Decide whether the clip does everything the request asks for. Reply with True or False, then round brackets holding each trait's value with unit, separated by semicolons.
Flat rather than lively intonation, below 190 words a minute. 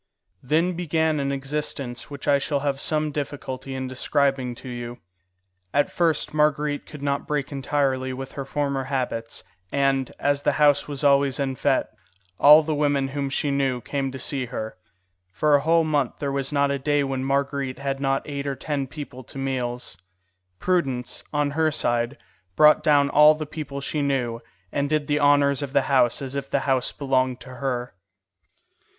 True (1.7 semitones; 180 wpm)